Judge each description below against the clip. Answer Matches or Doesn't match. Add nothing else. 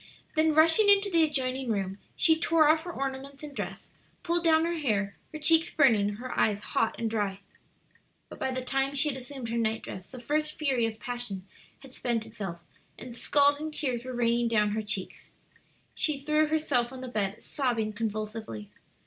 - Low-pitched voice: Doesn't match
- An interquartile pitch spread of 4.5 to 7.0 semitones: Matches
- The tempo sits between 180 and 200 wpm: Matches